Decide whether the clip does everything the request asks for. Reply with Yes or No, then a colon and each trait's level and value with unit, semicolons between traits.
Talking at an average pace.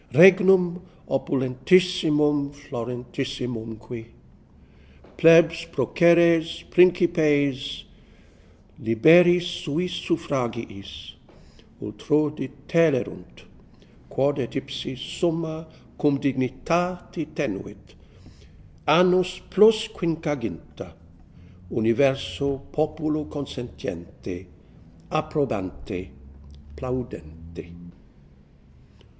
No: slow, 55 wpm